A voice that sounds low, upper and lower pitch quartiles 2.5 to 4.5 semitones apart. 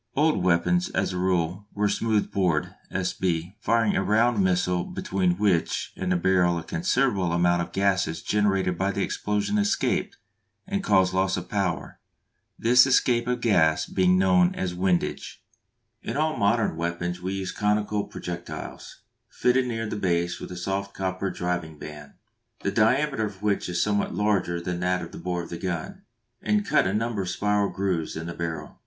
Yes: very low, 95 Hz; average, 3.0 semitones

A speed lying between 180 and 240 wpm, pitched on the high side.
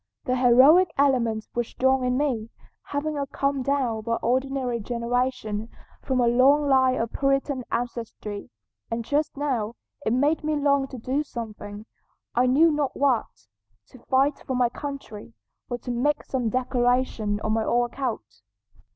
No: average, 150 wpm; very high, 255 Hz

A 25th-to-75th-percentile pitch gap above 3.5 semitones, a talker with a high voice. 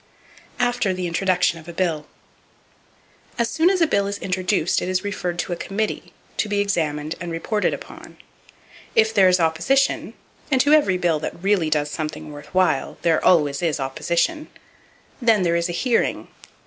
No: average, 4.1 semitones; medium, 180 Hz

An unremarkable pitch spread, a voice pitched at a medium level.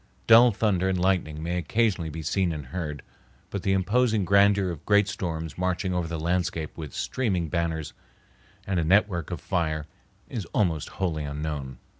No: average, 3.6 semitones; very low, 90 Hz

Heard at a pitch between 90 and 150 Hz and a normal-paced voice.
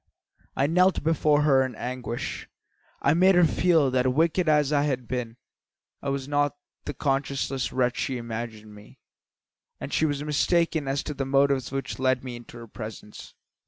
Yes: low, 135 Hz; average, 175 wpm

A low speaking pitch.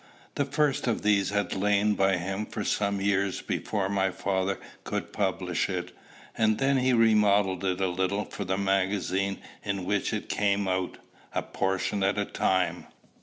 Yes: low, 100 Hz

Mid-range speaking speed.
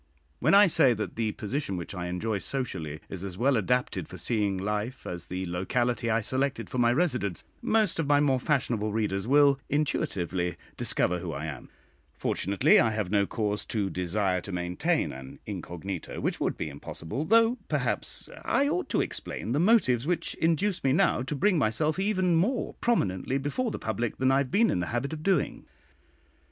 Yes: average, 185 wpm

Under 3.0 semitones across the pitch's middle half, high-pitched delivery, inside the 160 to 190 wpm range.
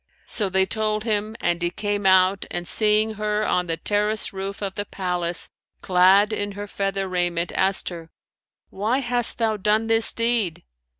Yes: narrow, 2.5 semitones; high, 205 Hz; average, 170 wpm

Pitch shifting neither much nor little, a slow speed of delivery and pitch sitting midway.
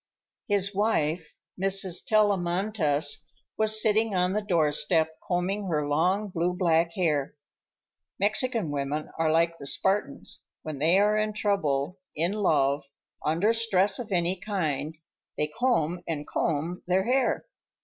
Yes: average, 4.7 semitones; slow, 130 wpm; medium, 180 Hz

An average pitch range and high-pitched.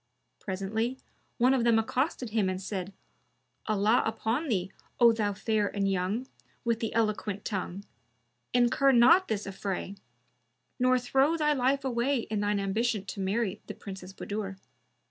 Yes: average, 3.8 semitones; high, 220 Hz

